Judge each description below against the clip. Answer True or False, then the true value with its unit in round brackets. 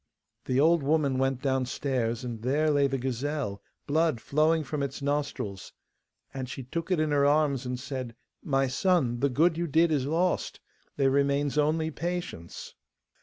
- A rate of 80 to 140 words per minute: False (165 wpm)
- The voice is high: False (140 Hz)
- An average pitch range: True (3.2 semitones)